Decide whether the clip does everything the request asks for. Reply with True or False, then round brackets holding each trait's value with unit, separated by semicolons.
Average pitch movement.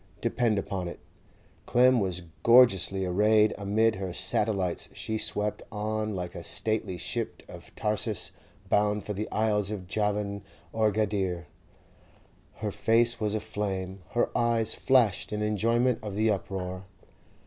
False (2.2 semitones)